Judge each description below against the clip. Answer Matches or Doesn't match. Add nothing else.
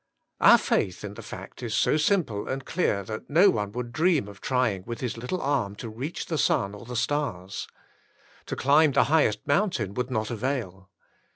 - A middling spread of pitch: Doesn't match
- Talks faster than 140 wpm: Matches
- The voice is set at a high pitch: Doesn't match